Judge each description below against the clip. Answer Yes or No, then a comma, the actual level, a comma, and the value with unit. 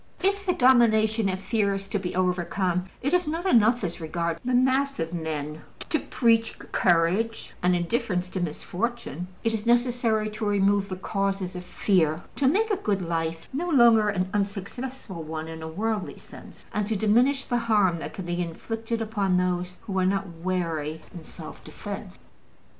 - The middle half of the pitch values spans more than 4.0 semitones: Yes, average, 4.7 semitones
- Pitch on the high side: Yes, high, 200 Hz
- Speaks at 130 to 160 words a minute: No, average, 175 wpm